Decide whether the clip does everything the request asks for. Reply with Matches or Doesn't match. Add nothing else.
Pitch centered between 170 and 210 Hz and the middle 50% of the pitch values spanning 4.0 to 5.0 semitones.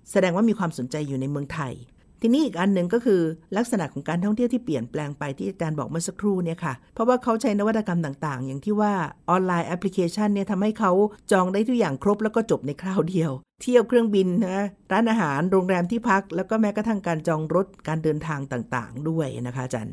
Doesn't match